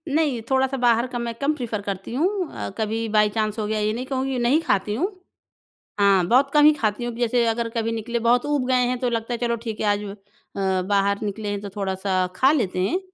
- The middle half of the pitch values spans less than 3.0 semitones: No, average, 3.4 semitones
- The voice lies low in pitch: No, high, 230 Hz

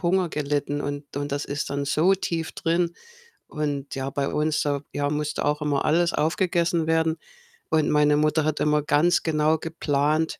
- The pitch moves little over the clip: Yes, narrow, 2.0 semitones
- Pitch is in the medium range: Yes, medium, 150 Hz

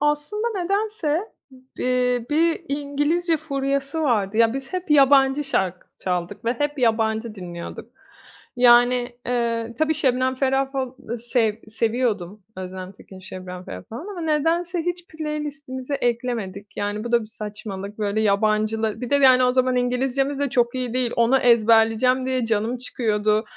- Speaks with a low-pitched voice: No, very high, 250 Hz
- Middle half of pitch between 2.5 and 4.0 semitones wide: No, average, 4.4 semitones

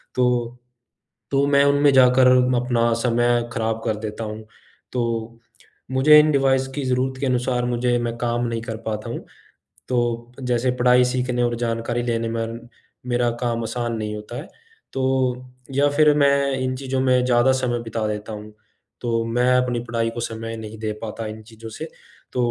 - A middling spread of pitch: No, narrow, 2.0 semitones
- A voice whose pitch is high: No, low, 120 Hz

